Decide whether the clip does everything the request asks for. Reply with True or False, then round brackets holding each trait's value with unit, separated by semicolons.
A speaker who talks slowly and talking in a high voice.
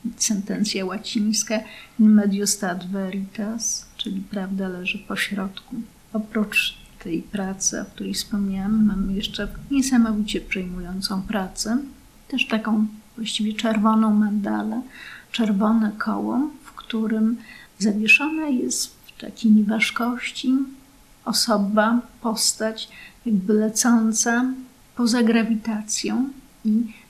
True (90 wpm; 220 Hz)